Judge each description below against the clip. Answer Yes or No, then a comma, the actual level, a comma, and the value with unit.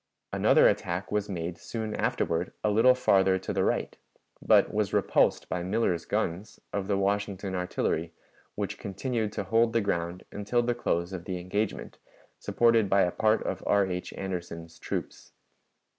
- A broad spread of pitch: No, average, 3.2 semitones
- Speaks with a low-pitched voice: Yes, low, 100 Hz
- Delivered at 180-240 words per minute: No, average, 160 wpm